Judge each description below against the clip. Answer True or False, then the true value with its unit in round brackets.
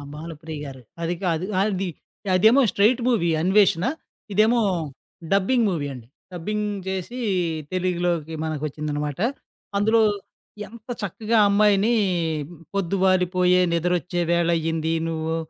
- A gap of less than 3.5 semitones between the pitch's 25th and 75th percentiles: False (4.1 semitones)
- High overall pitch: False (180 Hz)